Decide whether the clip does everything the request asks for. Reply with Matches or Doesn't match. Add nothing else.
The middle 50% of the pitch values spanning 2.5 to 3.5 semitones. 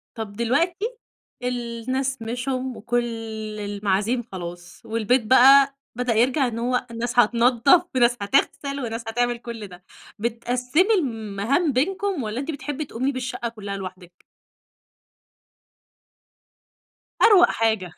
Matches